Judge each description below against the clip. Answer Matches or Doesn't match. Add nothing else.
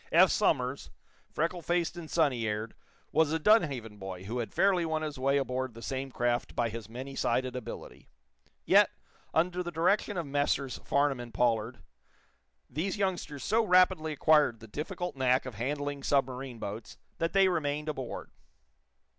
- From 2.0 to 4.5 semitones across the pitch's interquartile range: Doesn't match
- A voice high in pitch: Doesn't match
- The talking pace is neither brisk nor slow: Matches